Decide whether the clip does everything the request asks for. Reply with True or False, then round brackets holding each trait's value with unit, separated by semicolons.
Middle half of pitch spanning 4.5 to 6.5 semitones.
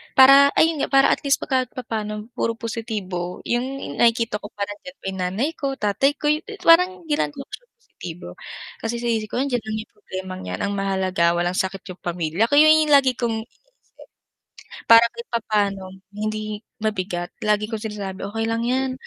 True (5.2 semitones)